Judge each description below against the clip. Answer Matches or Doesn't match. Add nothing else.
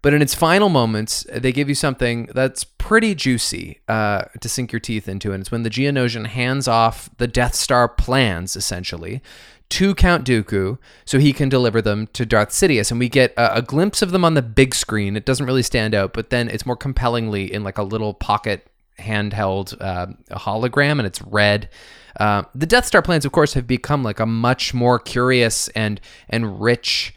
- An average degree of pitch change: Matches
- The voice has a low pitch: Matches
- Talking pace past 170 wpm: Matches